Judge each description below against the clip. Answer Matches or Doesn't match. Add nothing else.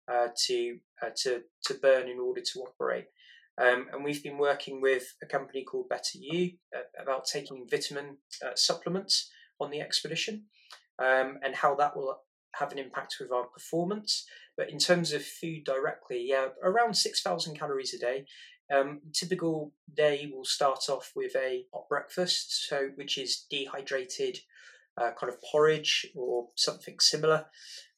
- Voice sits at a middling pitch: Matches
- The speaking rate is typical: Matches